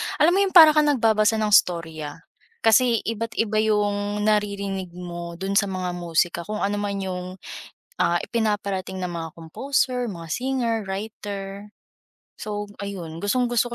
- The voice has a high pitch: Yes, high, 205 Hz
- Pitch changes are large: No, average, 3.7 semitones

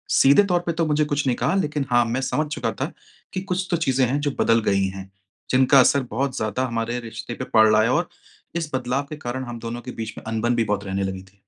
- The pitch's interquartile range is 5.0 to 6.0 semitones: No, average, 4.2 semitones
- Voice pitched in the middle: No, low, 125 Hz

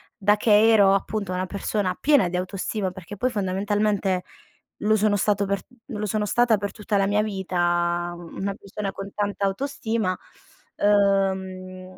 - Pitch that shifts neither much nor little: No, narrow, 2.1 semitones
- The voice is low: No, high, 200 Hz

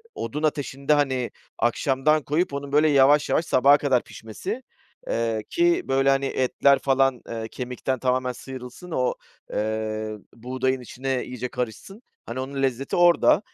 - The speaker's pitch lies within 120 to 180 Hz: Yes, low, 135 Hz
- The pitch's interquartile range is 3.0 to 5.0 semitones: No, narrow, 2.6 semitones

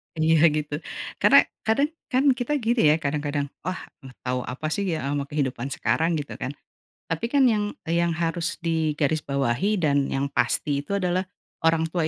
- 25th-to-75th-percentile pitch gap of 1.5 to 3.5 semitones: No, average, 4.3 semitones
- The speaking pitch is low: No, medium, 160 Hz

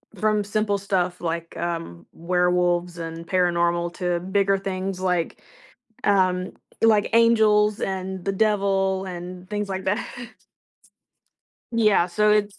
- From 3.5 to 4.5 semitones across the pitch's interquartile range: No, narrow, 2.5 semitones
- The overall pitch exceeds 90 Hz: Yes, high, 190 Hz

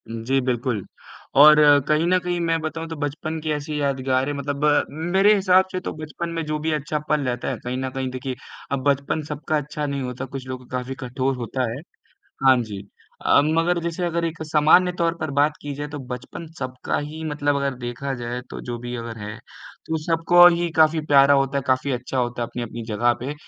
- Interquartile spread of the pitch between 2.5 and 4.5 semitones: Yes, average, 3.6 semitones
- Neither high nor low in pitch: Yes, medium, 145 Hz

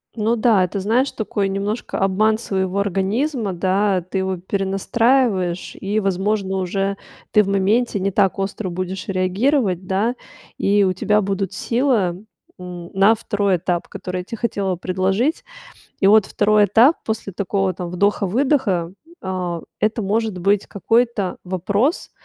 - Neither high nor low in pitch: No, high, 195 Hz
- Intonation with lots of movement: No, narrow, 2.6 semitones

